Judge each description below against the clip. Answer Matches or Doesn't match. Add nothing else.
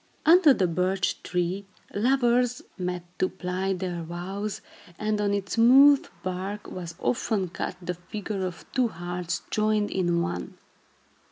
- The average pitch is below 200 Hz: Matches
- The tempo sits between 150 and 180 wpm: Doesn't match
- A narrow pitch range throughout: Doesn't match